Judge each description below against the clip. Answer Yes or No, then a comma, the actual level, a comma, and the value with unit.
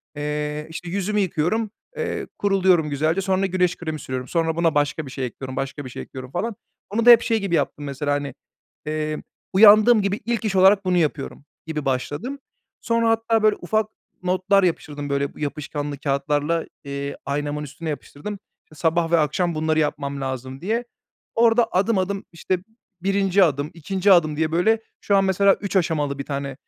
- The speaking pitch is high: No, medium, 165 Hz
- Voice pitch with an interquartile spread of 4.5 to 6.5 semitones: Yes, average, 5.2 semitones